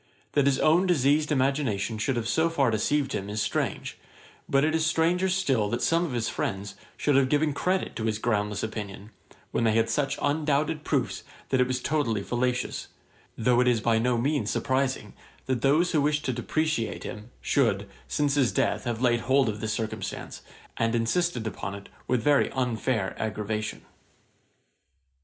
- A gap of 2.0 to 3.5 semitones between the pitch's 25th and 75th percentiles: No, average, 4.8 semitones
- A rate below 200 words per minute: Yes, average, 175 wpm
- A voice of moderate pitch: No, low, 125 Hz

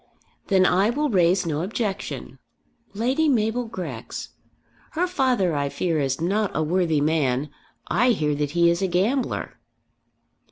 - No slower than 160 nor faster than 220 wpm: No, average, 145 wpm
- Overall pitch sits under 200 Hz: Yes, medium, 185 Hz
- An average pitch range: No, wide, 6.3 semitones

